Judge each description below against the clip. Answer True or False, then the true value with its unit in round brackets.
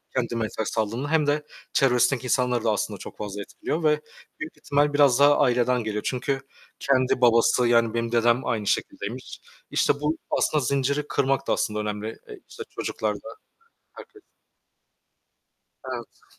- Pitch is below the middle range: True (125 Hz)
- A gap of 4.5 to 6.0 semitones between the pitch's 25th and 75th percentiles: False (3.7 semitones)